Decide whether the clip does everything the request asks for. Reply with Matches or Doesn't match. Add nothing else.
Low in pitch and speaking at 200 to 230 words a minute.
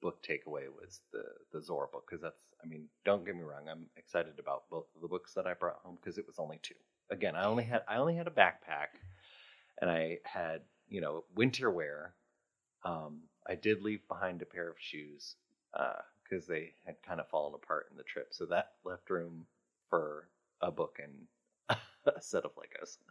Matches